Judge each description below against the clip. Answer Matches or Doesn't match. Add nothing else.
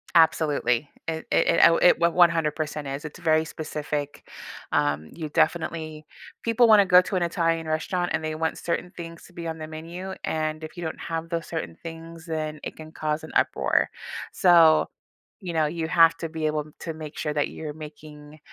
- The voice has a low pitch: Doesn't match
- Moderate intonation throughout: Doesn't match